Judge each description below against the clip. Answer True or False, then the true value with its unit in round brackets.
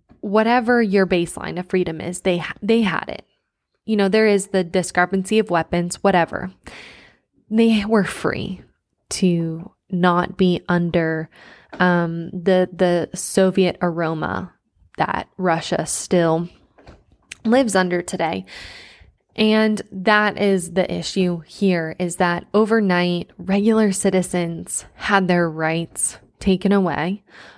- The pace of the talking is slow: True (115 wpm)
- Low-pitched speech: False (185 Hz)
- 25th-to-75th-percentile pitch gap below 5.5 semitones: True (2.5 semitones)